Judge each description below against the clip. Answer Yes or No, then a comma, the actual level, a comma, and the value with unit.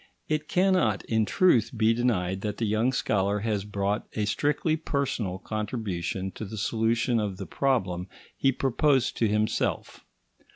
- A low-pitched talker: Yes, low, 110 Hz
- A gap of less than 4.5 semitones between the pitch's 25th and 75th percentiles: Yes, average, 3.9 semitones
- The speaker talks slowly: No, average, 150 wpm